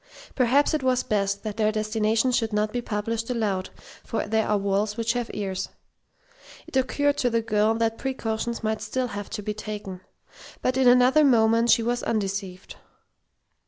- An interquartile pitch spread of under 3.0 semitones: Yes, narrow, 2.6 semitones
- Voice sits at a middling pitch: No, high, 220 Hz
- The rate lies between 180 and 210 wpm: No, average, 170 wpm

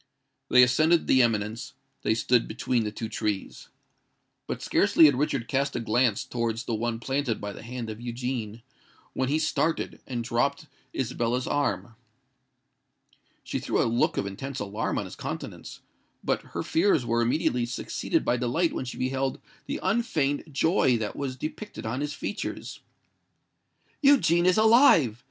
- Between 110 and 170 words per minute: Yes, average, 155 wpm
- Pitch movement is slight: No, average, 3.9 semitones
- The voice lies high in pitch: No, low, 125 Hz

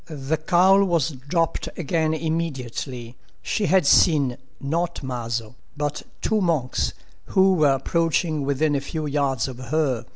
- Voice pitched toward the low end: No, medium, 150 Hz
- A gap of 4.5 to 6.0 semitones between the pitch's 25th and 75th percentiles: No, average, 4.0 semitones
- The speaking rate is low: Yes, slow, 130 wpm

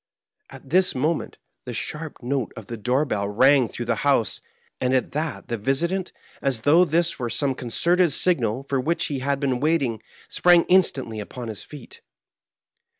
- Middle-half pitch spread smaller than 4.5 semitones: No, average, 5.0 semitones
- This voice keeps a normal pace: Yes, average, 160 wpm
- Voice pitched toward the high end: No, low, 135 Hz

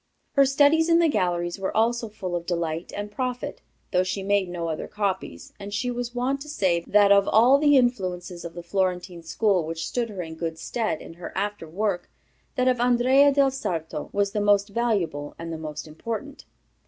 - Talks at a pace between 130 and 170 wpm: No, average, 200 wpm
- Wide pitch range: Yes, wide, 5.9 semitones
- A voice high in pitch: Yes, high, 200 Hz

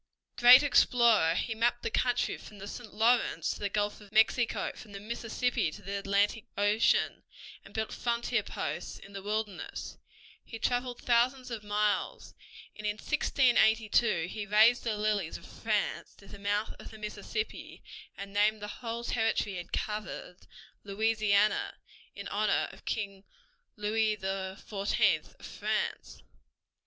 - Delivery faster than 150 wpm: No, average, 145 wpm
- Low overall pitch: No, high, 215 Hz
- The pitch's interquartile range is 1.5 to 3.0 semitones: Yes, narrow, 2.5 semitones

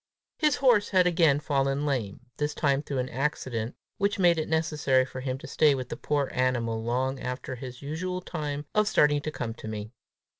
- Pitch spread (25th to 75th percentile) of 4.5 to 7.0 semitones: No, average, 3.8 semitones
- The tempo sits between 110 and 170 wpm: No, average, 195 wpm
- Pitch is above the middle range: No, medium, 140 Hz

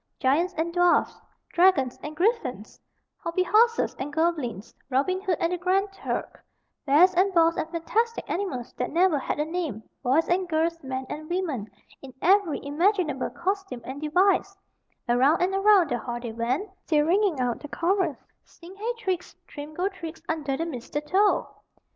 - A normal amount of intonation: Yes, average, 5.0 semitones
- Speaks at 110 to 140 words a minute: No, average, 165 wpm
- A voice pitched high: Yes, very high, 335 Hz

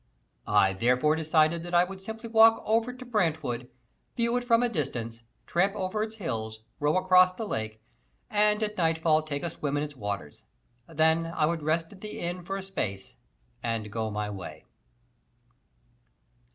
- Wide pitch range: Yes, wide, 8.2 semitones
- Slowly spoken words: No, average, 170 wpm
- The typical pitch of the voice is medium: Yes, medium, 165 Hz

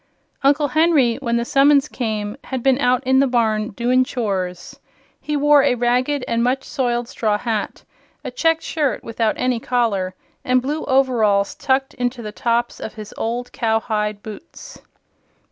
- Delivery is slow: No, average, 160 wpm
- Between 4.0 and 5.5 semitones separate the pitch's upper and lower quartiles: No, average, 3.4 semitones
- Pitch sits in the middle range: No, high, 245 Hz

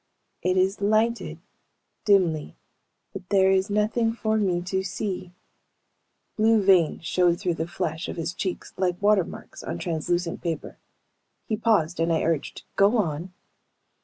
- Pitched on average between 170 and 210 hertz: Yes, medium, 185 Hz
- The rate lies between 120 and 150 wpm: Yes, average, 140 wpm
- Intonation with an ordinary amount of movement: Yes, average, 3.5 semitones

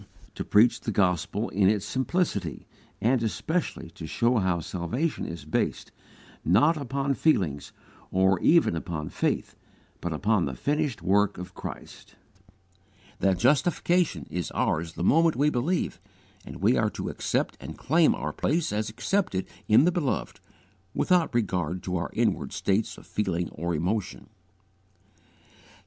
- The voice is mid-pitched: No, low, 105 Hz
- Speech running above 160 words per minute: No, average, 140 wpm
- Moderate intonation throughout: No, wide, 8.1 semitones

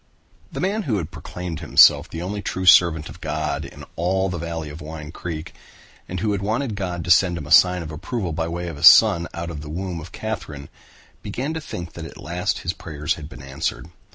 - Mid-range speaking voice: No, very low, 85 Hz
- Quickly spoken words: Yes, fast, 225 wpm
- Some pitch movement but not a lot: Yes, average, 3.2 semitones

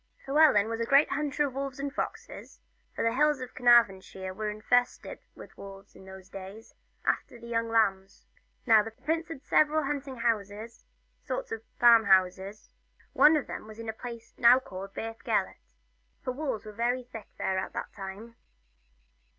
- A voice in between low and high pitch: No, high, 230 Hz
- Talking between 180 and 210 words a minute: Yes, average, 185 wpm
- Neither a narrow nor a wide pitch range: Yes, average, 4.7 semitones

